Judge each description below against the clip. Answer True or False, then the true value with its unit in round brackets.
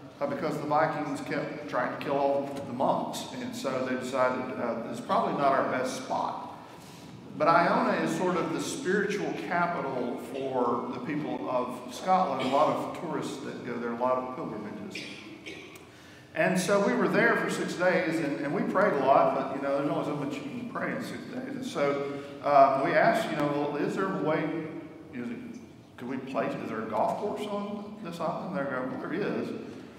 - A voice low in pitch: False (145 Hz)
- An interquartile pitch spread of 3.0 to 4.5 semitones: False (5.2 semitones)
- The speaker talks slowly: False (200 wpm)